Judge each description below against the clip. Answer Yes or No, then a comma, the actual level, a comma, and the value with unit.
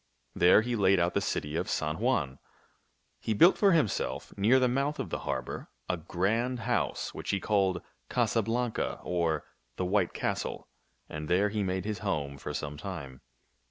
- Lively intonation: No, average, 4.7 semitones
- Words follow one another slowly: No, average, 175 wpm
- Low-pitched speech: Yes, very low, 95 Hz